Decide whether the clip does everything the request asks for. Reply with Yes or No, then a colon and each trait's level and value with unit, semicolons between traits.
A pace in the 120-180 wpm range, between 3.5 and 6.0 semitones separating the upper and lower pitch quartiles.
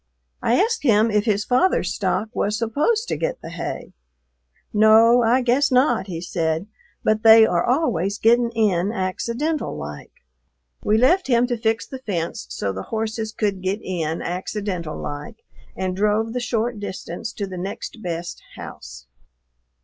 Yes: average, 155 wpm; average, 4.5 semitones